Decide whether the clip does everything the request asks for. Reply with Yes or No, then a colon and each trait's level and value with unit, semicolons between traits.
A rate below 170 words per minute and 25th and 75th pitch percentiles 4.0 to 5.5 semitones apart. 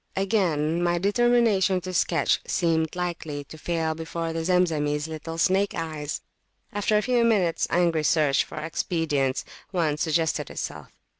No: average, 140 wpm; average, 2.9 semitones